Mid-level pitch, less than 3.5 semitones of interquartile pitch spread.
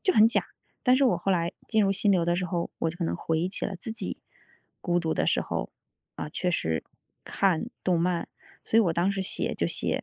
Yes: medium, 180 Hz; average, 2.8 semitones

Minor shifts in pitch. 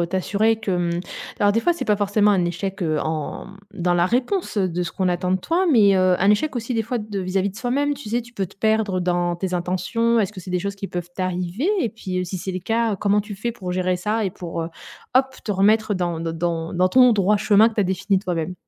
No: average, 3.6 semitones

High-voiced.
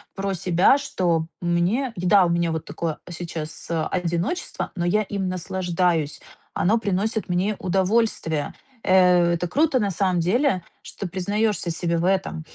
No: medium, 180 Hz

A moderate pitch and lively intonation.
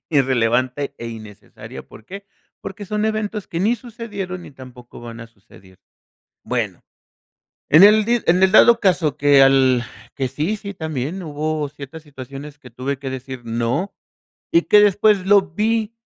Yes: medium, 150 Hz; wide, 7.6 semitones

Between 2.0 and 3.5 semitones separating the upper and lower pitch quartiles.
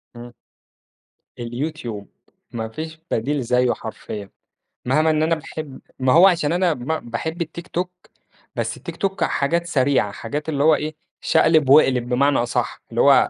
No: average, 4.7 semitones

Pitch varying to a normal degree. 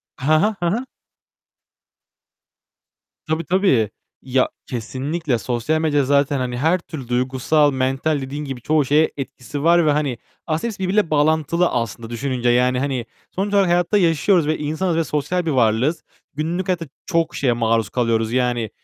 Yes: average, 4.7 semitones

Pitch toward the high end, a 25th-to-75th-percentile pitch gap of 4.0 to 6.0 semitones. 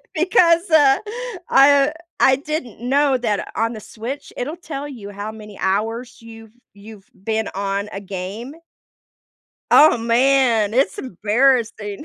Yes: high, 230 Hz; average, 4.7 semitones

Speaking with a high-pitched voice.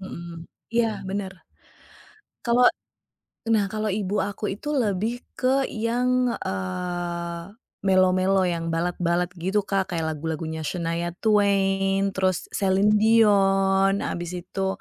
Yes: high, 195 Hz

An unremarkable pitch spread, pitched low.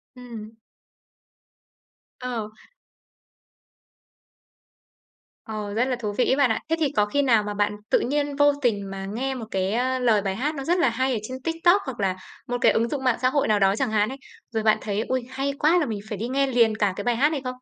No: average, 4.0 semitones; high, 245 Hz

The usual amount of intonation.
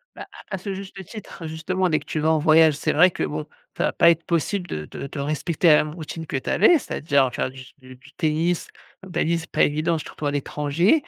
Yes: average, 3.1 semitones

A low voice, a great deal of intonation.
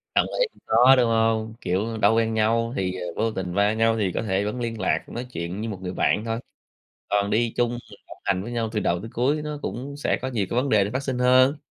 No: low, 115 Hz; average, 3.0 semitones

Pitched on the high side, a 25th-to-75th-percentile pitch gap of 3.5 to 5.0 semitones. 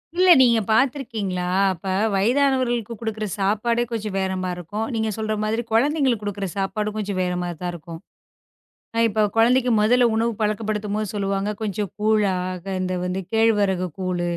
No: high, 215 Hz; average, 3.0 semitones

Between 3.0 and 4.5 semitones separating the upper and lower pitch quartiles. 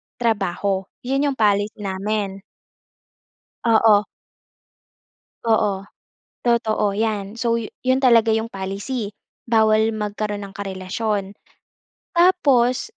No: narrow, 2.6 semitones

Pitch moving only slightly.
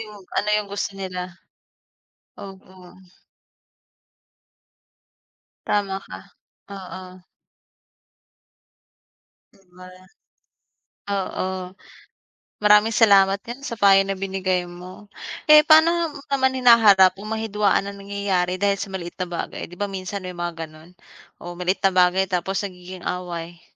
Yes: narrow, 2.2 semitones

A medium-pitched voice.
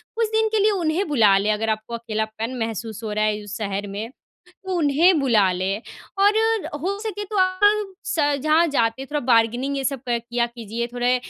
No: very high, 250 Hz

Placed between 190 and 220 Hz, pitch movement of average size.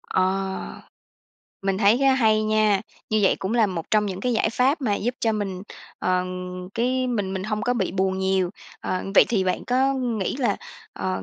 Yes: high, 210 Hz; average, 3.9 semitones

